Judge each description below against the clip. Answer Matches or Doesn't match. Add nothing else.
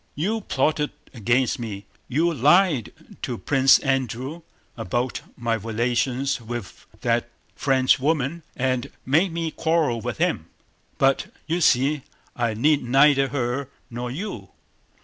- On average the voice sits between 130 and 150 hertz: Matches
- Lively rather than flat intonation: Doesn't match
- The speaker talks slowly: Matches